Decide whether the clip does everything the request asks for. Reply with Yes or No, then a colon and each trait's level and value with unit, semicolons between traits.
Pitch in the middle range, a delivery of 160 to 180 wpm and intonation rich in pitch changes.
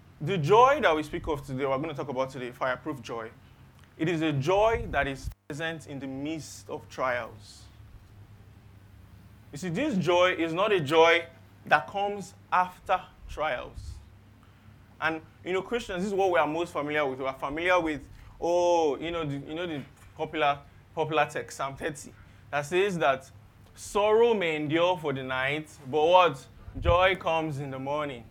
Yes: medium, 145 Hz; average, 175 wpm; wide, 7.0 semitones